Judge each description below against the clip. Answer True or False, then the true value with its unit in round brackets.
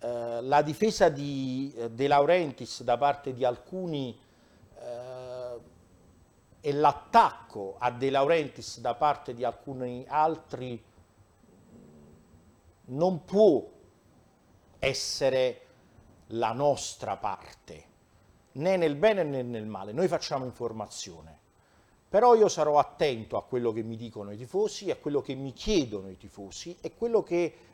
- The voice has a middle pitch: False (125 Hz)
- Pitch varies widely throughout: False (4.7 semitones)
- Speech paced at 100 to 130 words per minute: True (125 wpm)